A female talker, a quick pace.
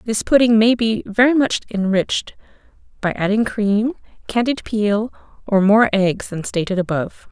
No: female; average, 150 wpm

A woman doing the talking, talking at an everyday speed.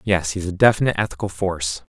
No: male; average, 185 wpm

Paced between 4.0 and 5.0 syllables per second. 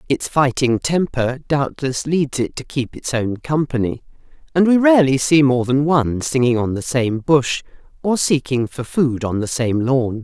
Yes: 4.5 syllables/s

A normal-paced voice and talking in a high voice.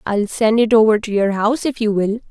No: fast, 260 wpm; high, 220 Hz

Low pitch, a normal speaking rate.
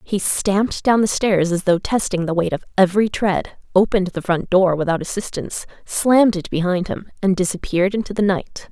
No: high, 190 Hz; average, 195 wpm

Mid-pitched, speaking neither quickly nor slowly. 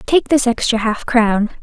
No: high, 240 Hz; average, 185 wpm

